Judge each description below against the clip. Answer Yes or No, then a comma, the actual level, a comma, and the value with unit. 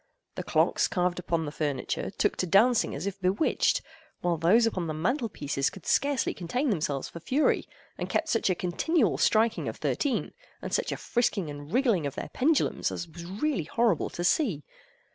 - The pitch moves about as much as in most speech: No, wide, 6.4 semitones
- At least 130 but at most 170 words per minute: No, average, 185 wpm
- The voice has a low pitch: No, medium, 185 Hz